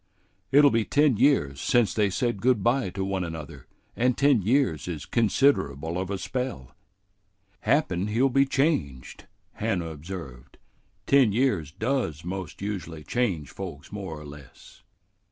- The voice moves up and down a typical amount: No, wide, 7.6 semitones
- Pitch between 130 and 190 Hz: No, low, 100 Hz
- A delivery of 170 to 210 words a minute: No, average, 140 wpm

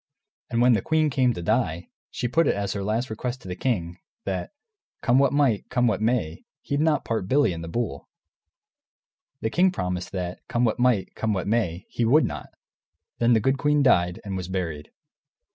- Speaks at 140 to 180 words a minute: No, fast, 205 wpm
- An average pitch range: No, wide, 5.7 semitones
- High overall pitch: No, low, 110 Hz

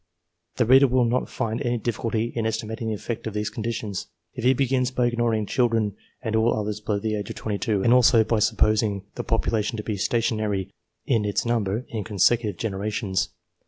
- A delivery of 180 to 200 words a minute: Yes, average, 195 wpm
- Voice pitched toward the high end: No, low, 110 Hz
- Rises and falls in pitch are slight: Yes, narrow, 2.1 semitones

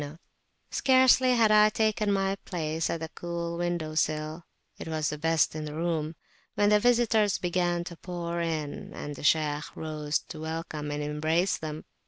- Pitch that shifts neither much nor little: Yes, average, 3.5 semitones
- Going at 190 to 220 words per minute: No, average, 170 wpm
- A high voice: No, medium, 165 Hz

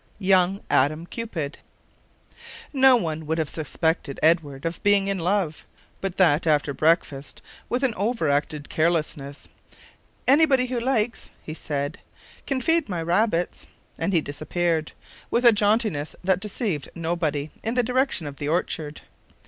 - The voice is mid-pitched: Yes, medium, 170 Hz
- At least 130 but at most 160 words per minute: Yes, average, 140 wpm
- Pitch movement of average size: No, wide, 5.8 semitones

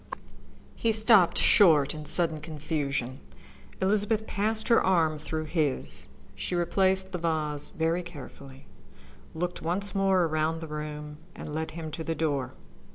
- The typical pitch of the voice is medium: Yes, medium, 160 Hz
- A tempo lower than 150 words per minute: Yes, average, 140 wpm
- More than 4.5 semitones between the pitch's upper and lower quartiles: No, average, 3.8 semitones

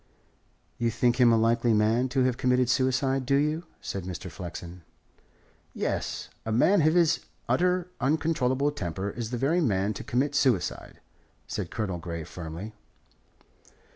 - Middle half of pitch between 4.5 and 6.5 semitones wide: Yes, average, 5.3 semitones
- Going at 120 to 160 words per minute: Yes, average, 145 wpm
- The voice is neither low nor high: No, low, 120 Hz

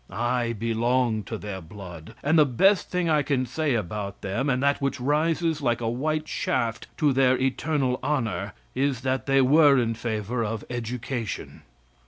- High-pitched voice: No, low, 125 Hz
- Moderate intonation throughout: Yes, average, 3.9 semitones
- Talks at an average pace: Yes, average, 170 wpm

